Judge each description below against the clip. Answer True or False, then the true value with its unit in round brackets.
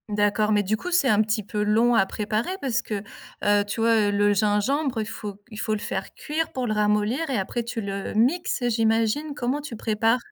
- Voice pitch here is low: False (220 Hz)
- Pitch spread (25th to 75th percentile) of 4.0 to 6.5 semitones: False (3.0 semitones)